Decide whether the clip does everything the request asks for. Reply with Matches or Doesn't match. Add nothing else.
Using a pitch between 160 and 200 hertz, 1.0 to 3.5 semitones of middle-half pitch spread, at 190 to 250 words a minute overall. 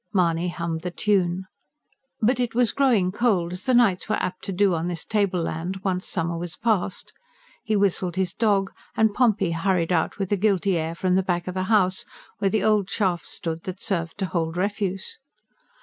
Matches